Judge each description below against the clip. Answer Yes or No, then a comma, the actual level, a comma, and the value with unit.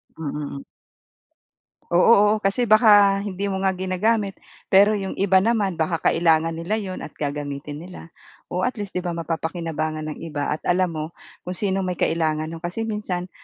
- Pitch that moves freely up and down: No, average, 3.5 semitones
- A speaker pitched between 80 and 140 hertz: No, medium, 180 Hz